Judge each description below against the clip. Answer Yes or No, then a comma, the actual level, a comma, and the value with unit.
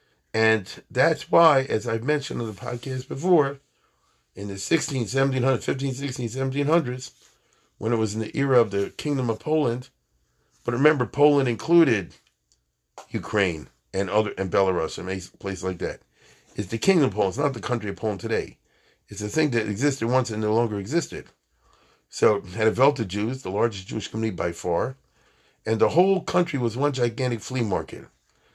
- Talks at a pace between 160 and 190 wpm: Yes, average, 175 wpm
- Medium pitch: No, low, 115 Hz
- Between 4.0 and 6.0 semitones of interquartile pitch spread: Yes, average, 4.4 semitones